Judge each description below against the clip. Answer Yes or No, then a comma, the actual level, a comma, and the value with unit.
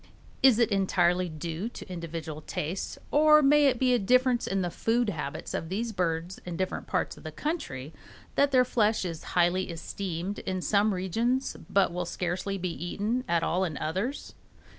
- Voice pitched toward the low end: No, high, 190 Hz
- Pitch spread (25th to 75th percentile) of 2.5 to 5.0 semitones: No, wide, 5.6 semitones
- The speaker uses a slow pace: No, average, 180 wpm